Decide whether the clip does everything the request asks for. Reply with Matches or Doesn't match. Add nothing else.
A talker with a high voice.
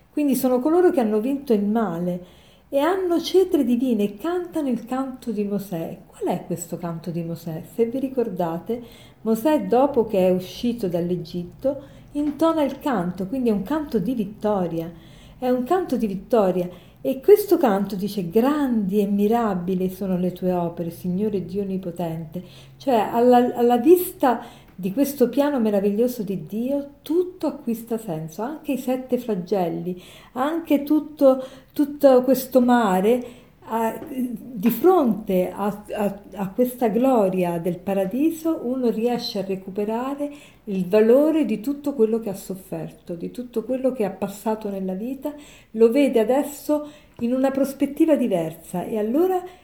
Matches